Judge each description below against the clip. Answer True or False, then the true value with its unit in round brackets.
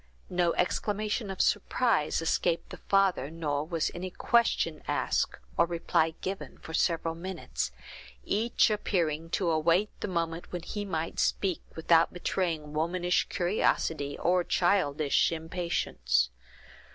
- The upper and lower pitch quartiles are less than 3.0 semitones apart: True (2.6 semitones)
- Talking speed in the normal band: False (125 wpm)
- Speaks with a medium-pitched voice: True (170 Hz)